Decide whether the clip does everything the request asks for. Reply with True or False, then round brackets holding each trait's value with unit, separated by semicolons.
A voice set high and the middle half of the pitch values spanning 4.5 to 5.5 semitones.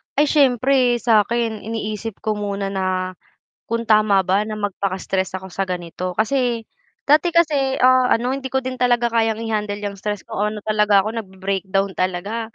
False (215 Hz; 3.7 semitones)